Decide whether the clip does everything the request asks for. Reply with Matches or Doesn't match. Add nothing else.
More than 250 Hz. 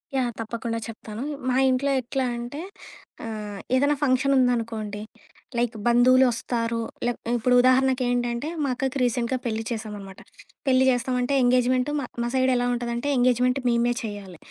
Doesn't match